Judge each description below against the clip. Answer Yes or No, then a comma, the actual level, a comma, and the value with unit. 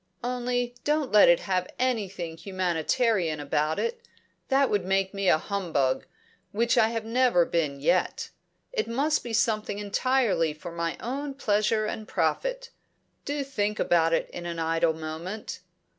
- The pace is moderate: Yes, average, 150 wpm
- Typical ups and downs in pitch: No, wide, 6.5 semitones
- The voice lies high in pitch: Yes, high, 205 Hz